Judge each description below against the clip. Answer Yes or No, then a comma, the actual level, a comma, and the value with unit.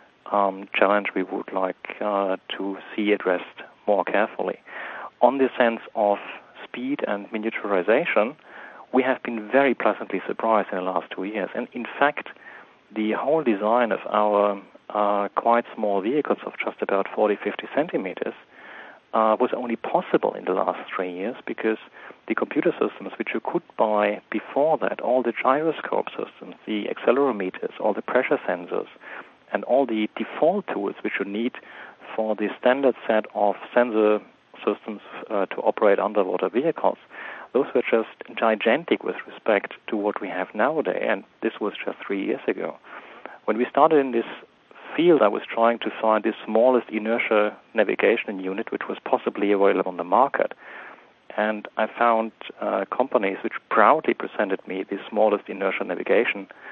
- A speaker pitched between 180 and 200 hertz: No, low, 110 Hz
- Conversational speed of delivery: Yes, average, 160 wpm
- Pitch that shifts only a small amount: Yes, narrow, 2.1 semitones